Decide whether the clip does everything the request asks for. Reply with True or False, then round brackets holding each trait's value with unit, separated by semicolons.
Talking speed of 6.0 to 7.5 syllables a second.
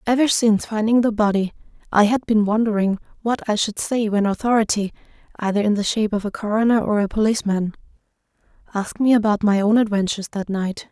True (6.2 syllables/s)